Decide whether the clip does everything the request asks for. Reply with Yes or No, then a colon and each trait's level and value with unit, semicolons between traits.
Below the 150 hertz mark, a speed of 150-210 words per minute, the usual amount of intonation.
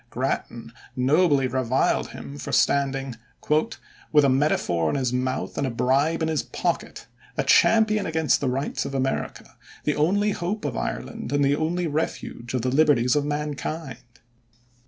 Yes: medium, 140 Hz; average, 155 wpm; average, 3.6 semitones